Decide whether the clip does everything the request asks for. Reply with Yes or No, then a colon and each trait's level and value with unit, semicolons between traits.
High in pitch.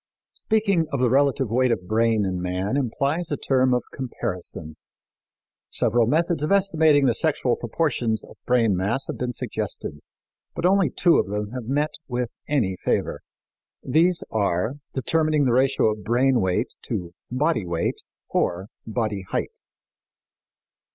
No: low, 125 Hz